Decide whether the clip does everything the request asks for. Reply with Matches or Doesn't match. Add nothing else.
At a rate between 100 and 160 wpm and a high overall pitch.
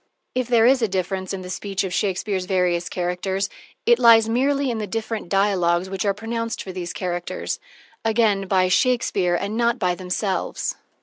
Doesn't match